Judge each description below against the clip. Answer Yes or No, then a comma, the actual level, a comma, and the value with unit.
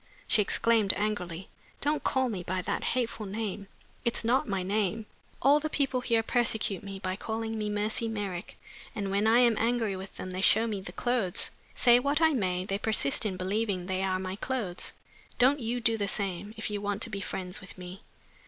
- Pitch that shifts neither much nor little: Yes, average, 3.3 semitones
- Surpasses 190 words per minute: Yes, average, 200 wpm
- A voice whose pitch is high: Yes, high, 210 Hz